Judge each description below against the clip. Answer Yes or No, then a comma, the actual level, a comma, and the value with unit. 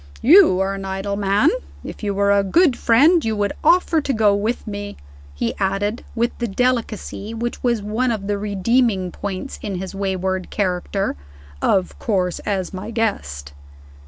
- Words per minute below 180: Yes, average, 165 wpm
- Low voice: No, high, 205 Hz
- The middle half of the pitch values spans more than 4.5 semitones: No, average, 3.3 semitones